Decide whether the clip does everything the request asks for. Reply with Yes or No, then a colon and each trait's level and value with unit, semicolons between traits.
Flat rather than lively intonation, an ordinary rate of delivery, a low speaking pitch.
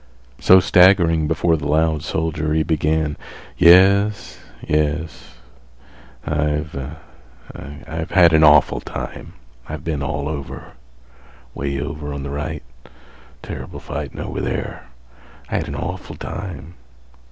No: narrow, 2.1 semitones; slow, 115 wpm; very low, 75 Hz